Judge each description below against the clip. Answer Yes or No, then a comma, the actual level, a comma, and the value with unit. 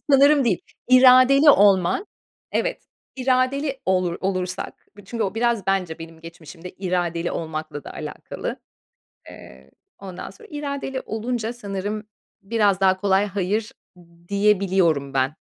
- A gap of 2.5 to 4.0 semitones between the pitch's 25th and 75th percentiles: No, wide, 5.4 semitones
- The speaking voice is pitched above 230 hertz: No, high, 195 Hz